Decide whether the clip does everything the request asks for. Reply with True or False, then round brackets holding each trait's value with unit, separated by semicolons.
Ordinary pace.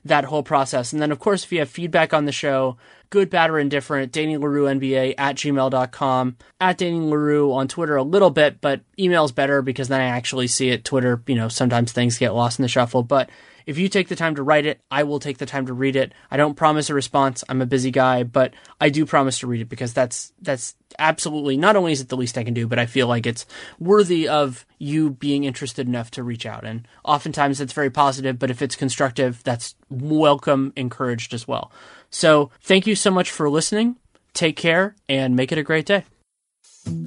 False (225 wpm)